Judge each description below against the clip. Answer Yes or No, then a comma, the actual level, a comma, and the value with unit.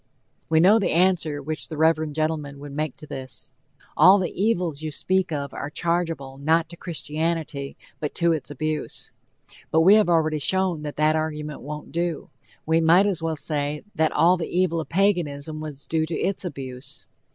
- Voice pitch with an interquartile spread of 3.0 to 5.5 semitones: No, narrow, 2.4 semitones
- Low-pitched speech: No, medium, 160 Hz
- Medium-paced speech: Yes, average, 185 wpm